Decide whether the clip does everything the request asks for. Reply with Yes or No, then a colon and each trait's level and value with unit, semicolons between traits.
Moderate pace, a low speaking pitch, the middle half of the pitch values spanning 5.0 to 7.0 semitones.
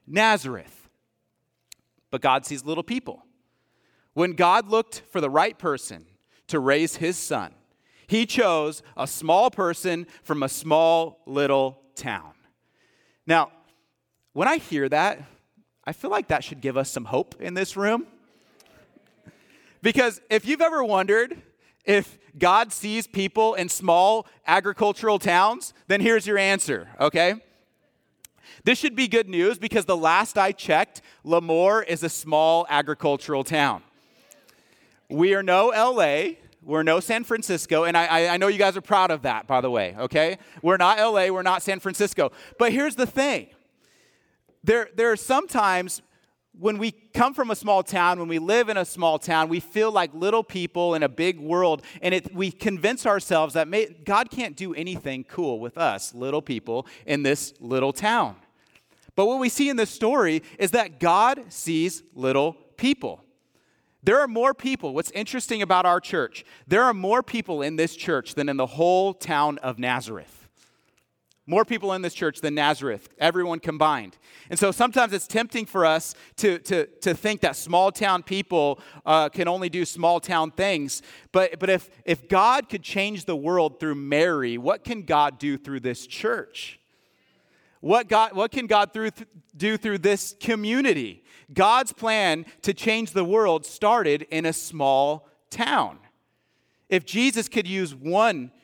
No: average, 165 wpm; medium, 180 Hz; wide, 5.5 semitones